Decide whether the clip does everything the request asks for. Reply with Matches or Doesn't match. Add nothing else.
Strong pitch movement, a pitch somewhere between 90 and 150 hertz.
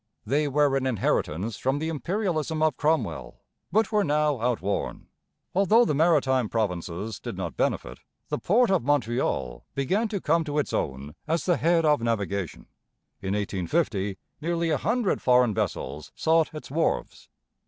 Matches